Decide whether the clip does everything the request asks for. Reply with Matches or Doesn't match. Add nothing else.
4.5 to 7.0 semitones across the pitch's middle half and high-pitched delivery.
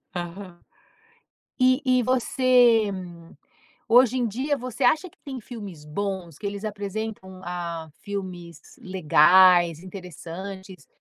Matches